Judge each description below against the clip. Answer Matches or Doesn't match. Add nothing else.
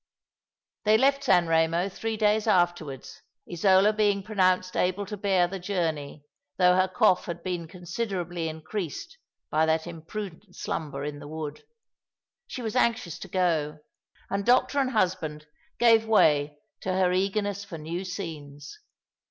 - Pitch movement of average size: Matches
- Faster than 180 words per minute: Doesn't match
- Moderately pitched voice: Matches